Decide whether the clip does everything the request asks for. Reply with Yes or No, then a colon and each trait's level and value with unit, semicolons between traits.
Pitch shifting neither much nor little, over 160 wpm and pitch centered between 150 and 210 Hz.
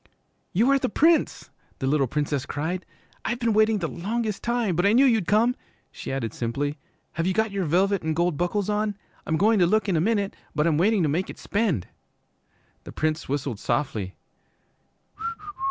No: wide, 6.1 semitones; average, 185 wpm; medium, 185 Hz